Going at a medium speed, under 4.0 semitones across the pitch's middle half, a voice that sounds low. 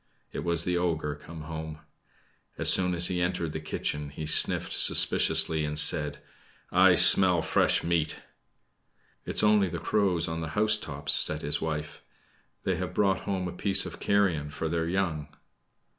Yes: average, 165 wpm; average, 2.9 semitones; very low, 85 Hz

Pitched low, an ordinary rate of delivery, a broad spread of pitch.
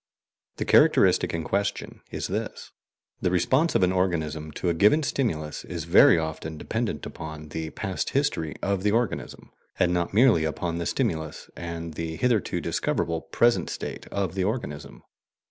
No: very low, 85 Hz; average, 160 wpm; average, 4.2 semitones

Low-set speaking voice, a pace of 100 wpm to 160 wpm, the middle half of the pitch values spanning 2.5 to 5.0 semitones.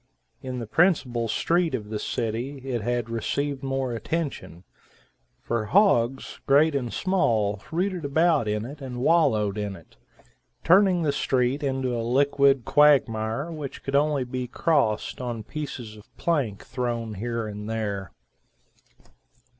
Yes: low, 125 Hz; average, 140 wpm; average, 4.5 semitones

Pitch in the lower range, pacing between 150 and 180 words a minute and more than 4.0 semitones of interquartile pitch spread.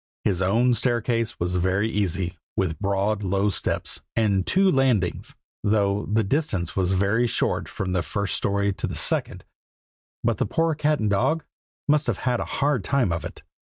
Yes: low, 105 Hz; average, 175 wpm; average, 4.4 semitones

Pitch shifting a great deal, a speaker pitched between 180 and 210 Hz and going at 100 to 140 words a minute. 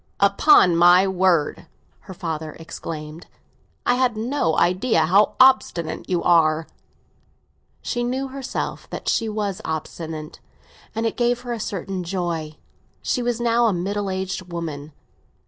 Yes: wide, 5.8 semitones; medium, 185 Hz; slow, 135 wpm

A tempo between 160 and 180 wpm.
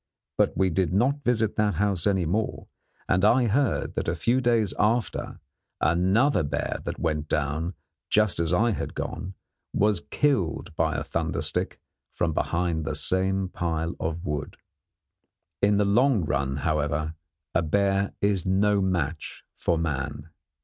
No: average, 150 wpm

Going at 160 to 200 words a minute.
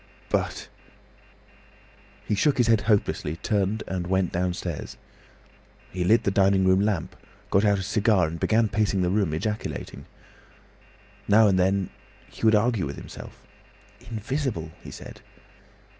No: average, 140 wpm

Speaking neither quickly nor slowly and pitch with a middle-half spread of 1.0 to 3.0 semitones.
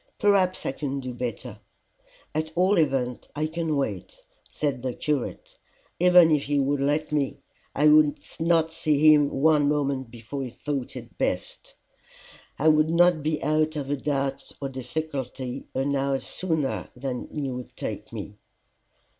Yes: average, 160 wpm; narrow, 2.6 semitones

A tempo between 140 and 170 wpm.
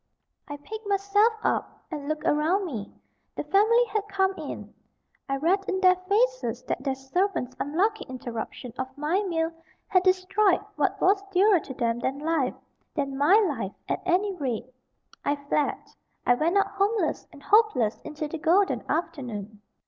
Yes: average, 160 wpm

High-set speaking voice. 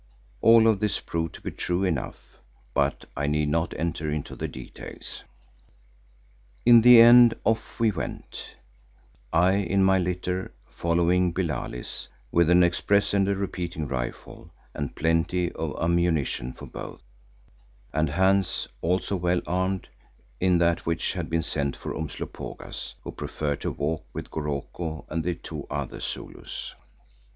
No: very low, 85 Hz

